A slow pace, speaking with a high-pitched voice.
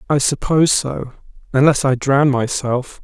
No: slow, 120 wpm; low, 135 Hz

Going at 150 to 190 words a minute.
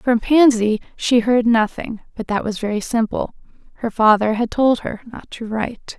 Yes: average, 180 wpm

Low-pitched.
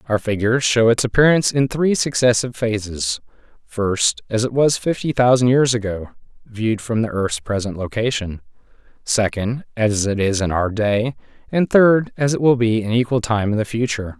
Yes: low, 115 Hz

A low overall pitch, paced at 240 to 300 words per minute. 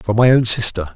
Yes: low, 110 Hz; fast, 250 wpm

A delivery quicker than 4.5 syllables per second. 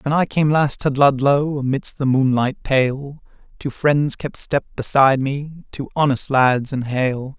No: 4.1 syllables/s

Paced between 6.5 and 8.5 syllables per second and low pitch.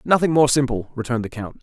Yes: 6.7 syllables/s; low, 130 Hz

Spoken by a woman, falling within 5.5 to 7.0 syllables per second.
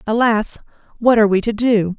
Yes: female; 5.6 syllables/s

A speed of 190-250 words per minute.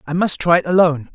No: fast, 260 wpm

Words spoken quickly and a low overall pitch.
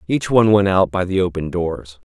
Yes: fast, 225 wpm; very low, 95 Hz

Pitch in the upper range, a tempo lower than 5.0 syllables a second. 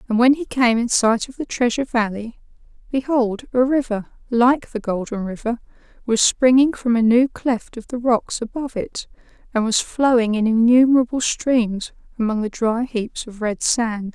Yes: high, 235 Hz; 4.7 syllables/s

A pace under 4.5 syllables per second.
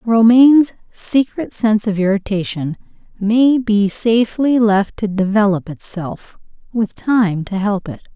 Yes: 4.1 syllables/s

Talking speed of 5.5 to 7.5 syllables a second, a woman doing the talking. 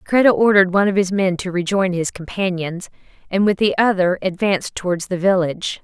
Yes: 5.9 syllables/s; female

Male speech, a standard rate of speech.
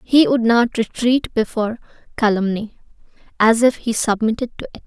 No: female; average, 150 wpm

